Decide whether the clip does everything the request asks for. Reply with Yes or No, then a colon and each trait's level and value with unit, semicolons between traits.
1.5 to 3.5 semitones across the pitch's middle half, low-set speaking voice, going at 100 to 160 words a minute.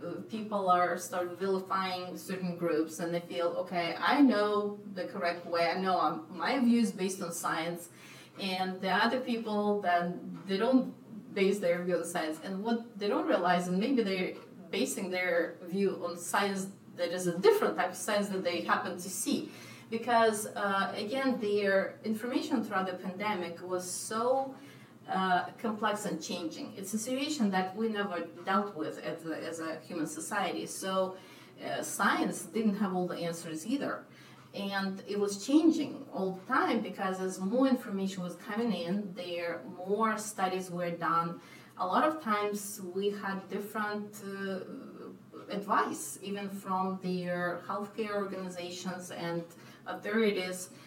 No: average, 3.2 semitones; high, 190 Hz; average, 155 wpm